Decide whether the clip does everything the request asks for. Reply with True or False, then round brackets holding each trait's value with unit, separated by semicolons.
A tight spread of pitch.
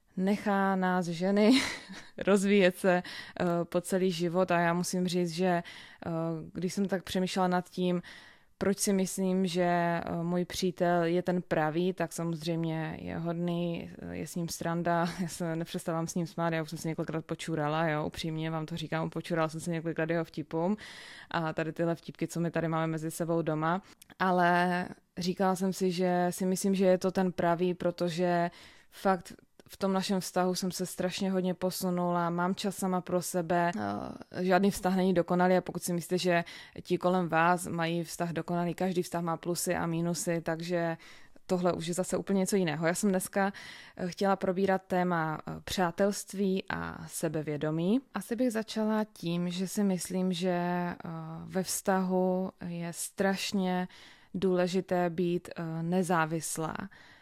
True (1.9 semitones)